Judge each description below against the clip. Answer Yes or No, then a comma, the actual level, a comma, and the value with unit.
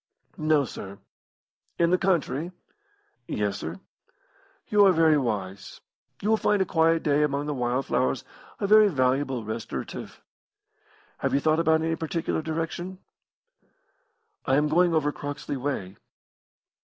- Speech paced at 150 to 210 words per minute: No, slow, 135 wpm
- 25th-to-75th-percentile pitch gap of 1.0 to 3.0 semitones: No, average, 4.0 semitones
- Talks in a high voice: No, medium, 150 Hz